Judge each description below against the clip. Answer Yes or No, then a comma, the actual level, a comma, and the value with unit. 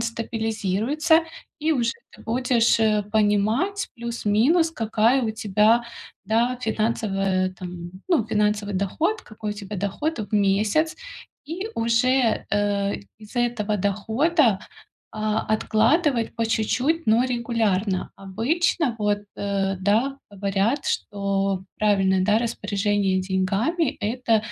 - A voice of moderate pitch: No, high, 220 Hz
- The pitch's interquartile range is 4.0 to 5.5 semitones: No, average, 3.2 semitones